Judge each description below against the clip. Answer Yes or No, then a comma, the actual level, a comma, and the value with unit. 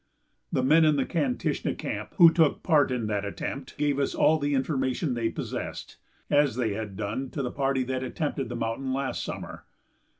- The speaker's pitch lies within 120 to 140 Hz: Yes, low, 135 Hz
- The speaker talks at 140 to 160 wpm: No, average, 190 wpm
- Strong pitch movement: No, average, 3.3 semitones